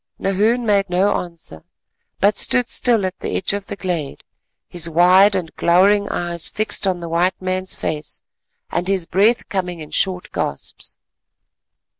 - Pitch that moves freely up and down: No, average, 2.7 semitones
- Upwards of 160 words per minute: No, average, 155 wpm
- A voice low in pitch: No, medium, 185 Hz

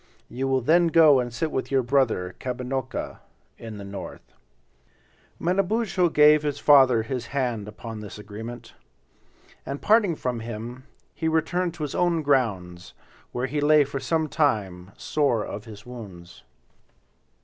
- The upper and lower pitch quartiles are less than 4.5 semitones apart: No, average, 5.3 semitones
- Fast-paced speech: No, average, 145 wpm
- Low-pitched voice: Yes, low, 130 Hz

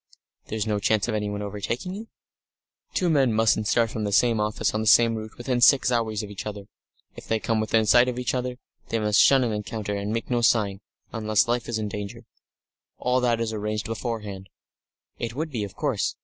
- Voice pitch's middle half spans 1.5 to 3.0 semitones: Yes, narrow, 2.4 semitones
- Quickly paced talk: Yes, fast, 210 wpm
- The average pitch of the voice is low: Yes, low, 110 Hz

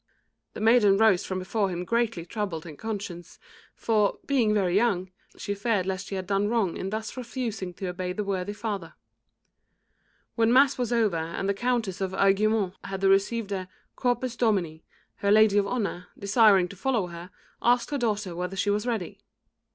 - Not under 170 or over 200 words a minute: Yes, average, 175 wpm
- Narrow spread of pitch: No, average, 3.3 semitones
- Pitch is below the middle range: No, high, 200 Hz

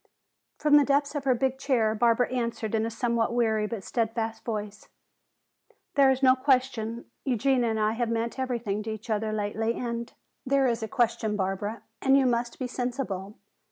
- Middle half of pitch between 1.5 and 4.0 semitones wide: Yes, average, 2.8 semitones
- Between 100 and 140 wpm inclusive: No, average, 185 wpm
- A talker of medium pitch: No, high, 235 Hz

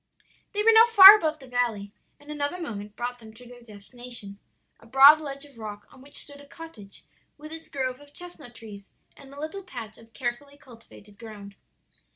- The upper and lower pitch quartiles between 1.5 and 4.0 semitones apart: No, average, 4.9 semitones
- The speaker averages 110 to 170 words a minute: No, average, 190 wpm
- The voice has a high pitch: Yes, very high, 255 Hz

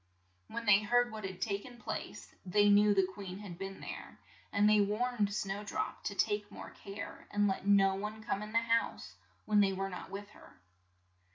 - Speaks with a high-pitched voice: Yes, high, 205 Hz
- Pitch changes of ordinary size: No, narrow, 1.5 semitones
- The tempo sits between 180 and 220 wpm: Yes, average, 200 wpm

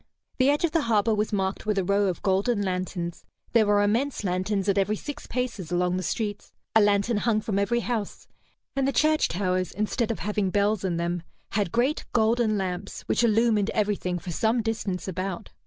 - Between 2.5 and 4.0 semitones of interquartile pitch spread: Yes, average, 3.3 semitones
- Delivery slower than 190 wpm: No, average, 195 wpm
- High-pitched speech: Yes, high, 205 Hz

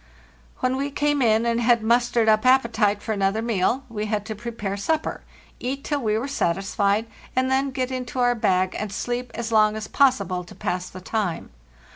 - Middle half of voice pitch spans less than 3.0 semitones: No, average, 3.5 semitones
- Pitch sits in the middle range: No, high, 230 Hz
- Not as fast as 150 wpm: No, average, 190 wpm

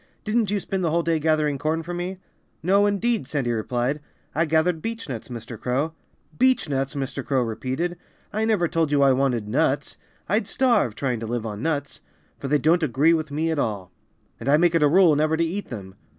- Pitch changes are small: No, average, 4.9 semitones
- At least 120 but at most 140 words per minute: No, fast, 205 wpm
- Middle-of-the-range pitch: Yes, medium, 155 Hz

